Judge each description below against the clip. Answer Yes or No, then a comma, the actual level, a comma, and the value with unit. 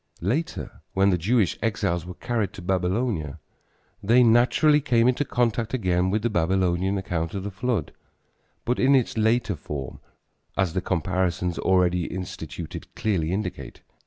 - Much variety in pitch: No, average, 4.7 semitones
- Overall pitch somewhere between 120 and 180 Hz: No, very low, 95 Hz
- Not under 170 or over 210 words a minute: No, average, 145 wpm